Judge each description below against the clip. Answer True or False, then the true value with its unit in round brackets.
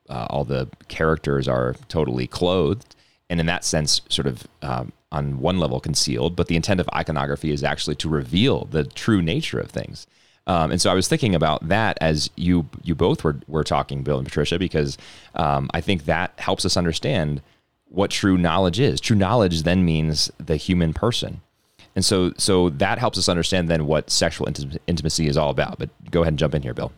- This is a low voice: True (80 Hz)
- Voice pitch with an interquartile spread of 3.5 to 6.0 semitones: True (3.8 semitones)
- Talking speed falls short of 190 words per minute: False (200 wpm)